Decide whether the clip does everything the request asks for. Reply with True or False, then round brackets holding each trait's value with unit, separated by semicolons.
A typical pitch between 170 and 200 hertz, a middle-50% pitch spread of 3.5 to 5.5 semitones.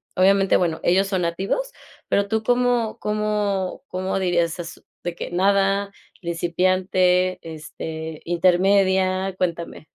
False (185 Hz; 2.4 semitones)